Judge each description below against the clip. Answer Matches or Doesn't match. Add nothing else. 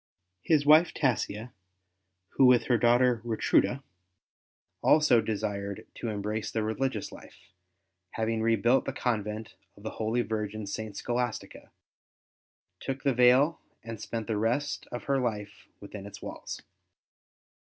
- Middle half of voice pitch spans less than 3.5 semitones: Matches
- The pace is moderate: Doesn't match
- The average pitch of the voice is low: Matches